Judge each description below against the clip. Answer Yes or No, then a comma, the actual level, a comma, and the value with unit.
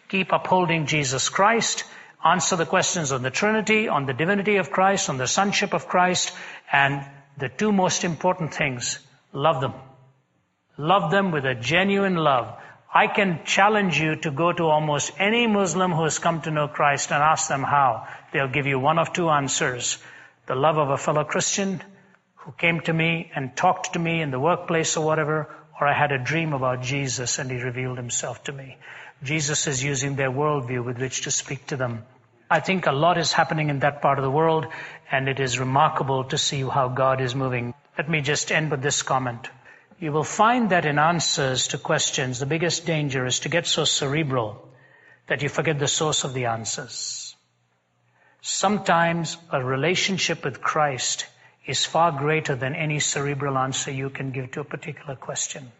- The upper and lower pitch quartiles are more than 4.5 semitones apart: No, average, 3.8 semitones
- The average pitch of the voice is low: No, medium, 150 Hz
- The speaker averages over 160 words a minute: Yes, average, 190 wpm